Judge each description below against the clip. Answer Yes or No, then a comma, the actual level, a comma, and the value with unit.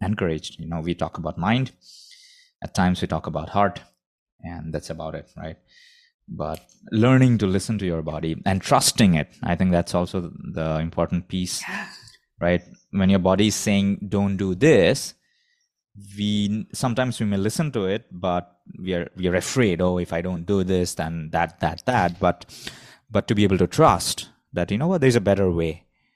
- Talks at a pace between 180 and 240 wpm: Yes, average, 185 wpm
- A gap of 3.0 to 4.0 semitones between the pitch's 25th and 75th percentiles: Yes, average, 3.3 semitones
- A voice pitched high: No, very low, 95 Hz